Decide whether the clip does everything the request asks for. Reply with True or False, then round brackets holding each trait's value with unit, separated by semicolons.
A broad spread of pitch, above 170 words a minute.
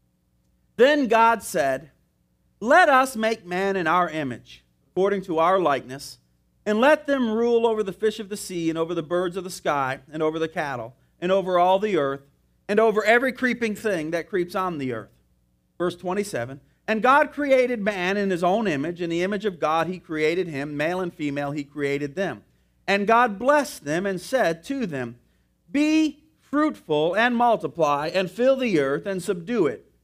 True (7.4 semitones; 185 wpm)